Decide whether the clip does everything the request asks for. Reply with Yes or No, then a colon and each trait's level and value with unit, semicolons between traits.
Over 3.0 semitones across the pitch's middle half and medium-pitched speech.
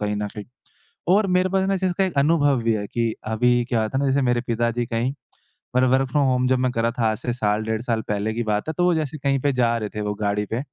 No: average, 4.0 semitones; low, 120 Hz